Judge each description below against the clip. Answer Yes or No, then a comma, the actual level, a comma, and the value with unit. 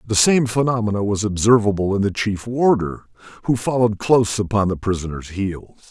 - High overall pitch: No, low, 105 Hz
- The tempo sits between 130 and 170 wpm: Yes, average, 165 wpm